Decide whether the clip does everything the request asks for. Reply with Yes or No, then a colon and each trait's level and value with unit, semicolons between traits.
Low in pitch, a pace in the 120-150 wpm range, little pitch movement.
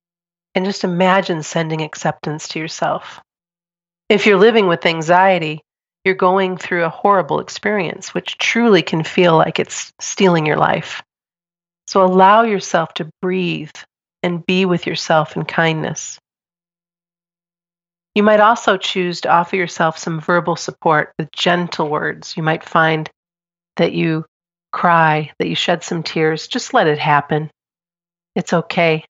No: medium, 175 Hz; average, 140 wpm; narrow, 2.3 semitones